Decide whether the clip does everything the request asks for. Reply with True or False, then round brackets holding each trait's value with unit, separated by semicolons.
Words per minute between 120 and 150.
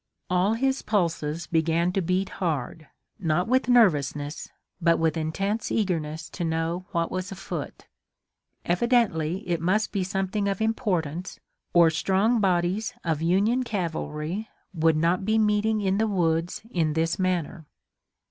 True (140 wpm)